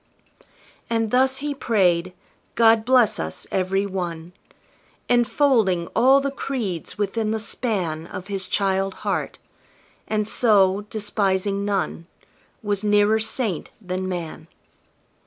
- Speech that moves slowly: Yes, slow, 115 wpm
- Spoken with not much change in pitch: No, average, 3.4 semitones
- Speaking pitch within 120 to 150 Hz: No, high, 205 Hz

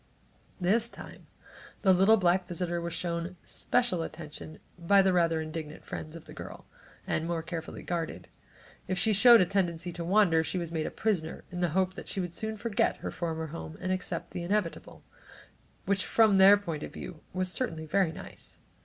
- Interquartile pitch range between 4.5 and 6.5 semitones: No, average, 2.9 semitones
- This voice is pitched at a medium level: Yes, medium, 175 Hz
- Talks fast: No, average, 190 wpm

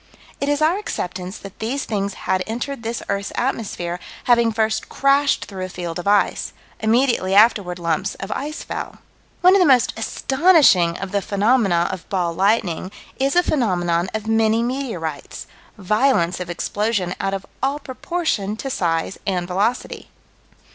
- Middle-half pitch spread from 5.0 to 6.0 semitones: Yes, wide, 5.6 semitones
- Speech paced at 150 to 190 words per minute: Yes, average, 155 wpm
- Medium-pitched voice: No, high, 210 Hz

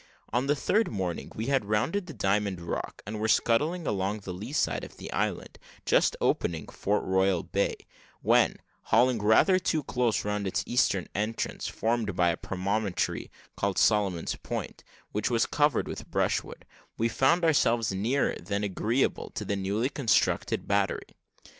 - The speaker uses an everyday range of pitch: Yes, average, 4.3 semitones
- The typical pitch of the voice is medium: No, low, 105 Hz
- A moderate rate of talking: Yes, average, 160 wpm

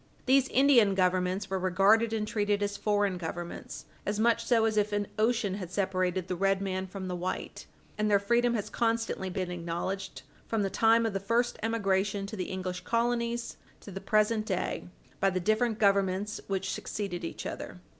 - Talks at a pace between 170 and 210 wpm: Yes, average, 185 wpm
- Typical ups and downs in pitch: Yes, average, 3.1 semitones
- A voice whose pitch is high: Yes, high, 200 Hz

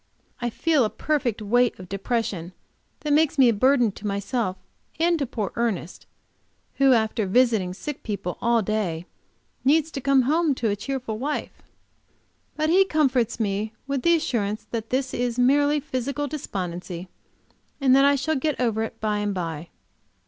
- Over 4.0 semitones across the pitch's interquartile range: Yes, average, 5.2 semitones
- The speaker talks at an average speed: Yes, average, 165 wpm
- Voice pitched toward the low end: No, high, 240 Hz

